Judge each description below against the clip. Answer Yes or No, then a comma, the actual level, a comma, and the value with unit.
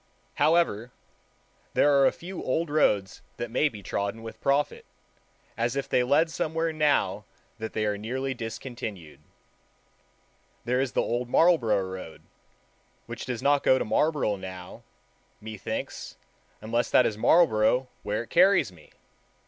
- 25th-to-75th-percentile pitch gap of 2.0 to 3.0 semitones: No, wide, 5.4 semitones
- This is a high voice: No, low, 120 Hz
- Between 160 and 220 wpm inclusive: No, average, 140 wpm